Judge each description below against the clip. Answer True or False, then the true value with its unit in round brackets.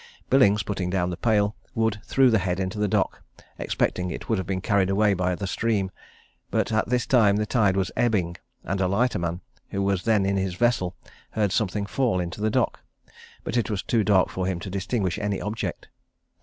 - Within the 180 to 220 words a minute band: True (205 wpm)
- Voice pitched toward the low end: True (100 Hz)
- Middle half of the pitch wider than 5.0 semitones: False (2.8 semitones)